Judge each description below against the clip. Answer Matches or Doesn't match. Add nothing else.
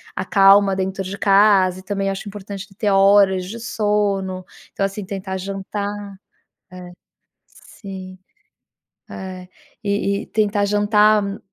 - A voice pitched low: Doesn't match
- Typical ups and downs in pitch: Doesn't match